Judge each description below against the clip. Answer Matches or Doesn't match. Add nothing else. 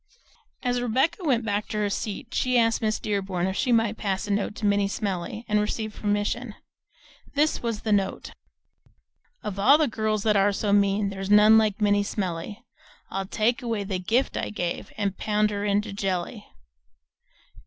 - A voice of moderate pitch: Doesn't match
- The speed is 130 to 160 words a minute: Doesn't match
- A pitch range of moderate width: Doesn't match